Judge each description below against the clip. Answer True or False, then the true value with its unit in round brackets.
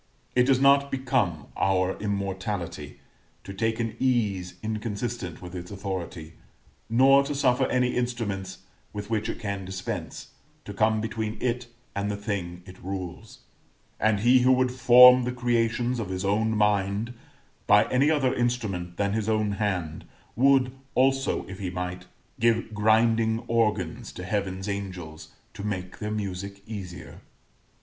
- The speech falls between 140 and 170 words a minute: True (145 wpm)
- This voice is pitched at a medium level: False (105 Hz)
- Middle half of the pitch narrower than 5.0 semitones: True (4.1 semitones)